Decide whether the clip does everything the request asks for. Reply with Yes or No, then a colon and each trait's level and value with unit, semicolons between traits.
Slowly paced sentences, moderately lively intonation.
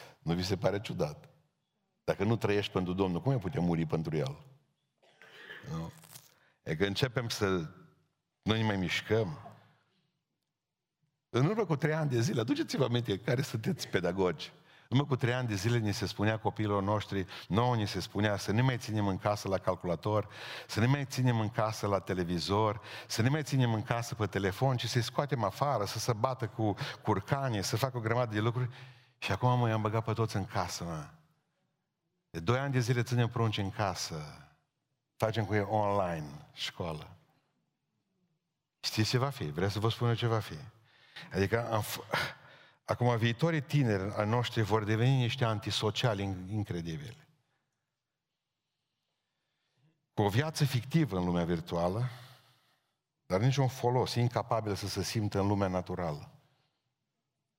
No: average, 165 wpm; average, 4.8 semitones